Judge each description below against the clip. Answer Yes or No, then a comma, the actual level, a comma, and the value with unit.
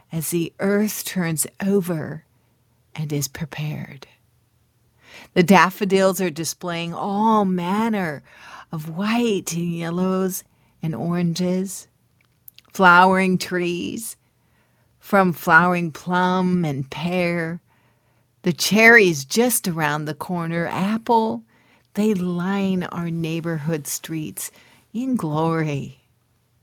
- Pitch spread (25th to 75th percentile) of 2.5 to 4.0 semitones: Yes, average, 3.7 semitones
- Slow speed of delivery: Yes, slow, 90 wpm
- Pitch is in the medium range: Yes, medium, 175 Hz